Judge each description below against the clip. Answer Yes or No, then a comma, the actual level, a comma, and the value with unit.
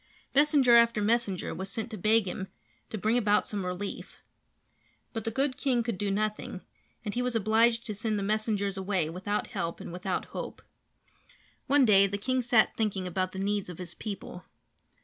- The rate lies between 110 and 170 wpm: No, average, 185 wpm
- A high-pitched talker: Yes, high, 210 Hz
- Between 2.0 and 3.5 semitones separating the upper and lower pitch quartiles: Yes, average, 3.2 semitones